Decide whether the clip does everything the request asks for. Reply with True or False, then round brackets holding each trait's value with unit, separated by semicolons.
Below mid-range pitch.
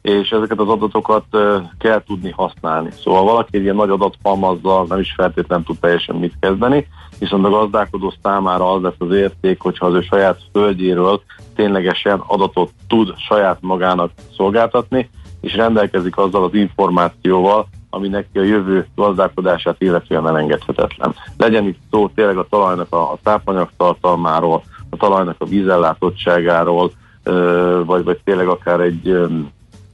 True (95 Hz)